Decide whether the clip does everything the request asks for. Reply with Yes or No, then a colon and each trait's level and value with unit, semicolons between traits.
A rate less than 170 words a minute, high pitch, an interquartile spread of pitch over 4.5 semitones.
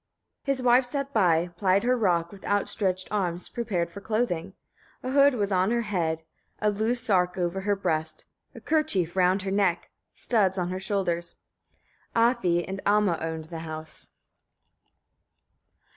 No: average, 155 wpm; high, 195 Hz; average, 4.2 semitones